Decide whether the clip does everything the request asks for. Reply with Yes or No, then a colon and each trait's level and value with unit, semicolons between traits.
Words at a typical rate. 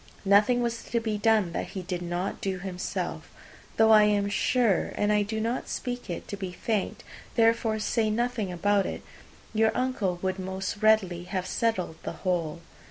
Yes: average, 175 wpm